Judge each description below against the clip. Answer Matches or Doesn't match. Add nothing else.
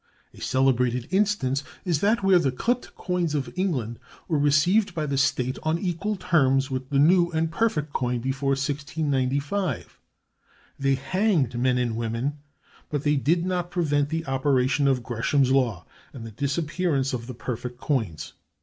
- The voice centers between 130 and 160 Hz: Matches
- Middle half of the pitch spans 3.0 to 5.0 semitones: Matches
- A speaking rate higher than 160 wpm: Doesn't match